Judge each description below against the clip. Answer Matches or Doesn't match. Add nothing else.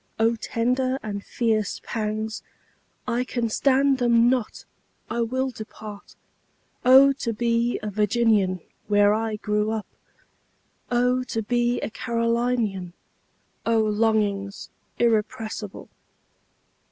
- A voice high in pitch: Matches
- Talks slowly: Matches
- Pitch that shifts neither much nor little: Doesn't match